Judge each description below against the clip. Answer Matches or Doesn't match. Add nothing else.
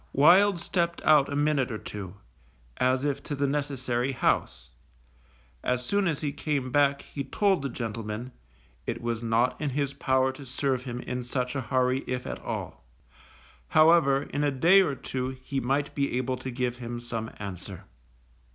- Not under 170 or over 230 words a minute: Matches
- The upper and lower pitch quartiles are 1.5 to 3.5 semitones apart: Matches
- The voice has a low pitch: Matches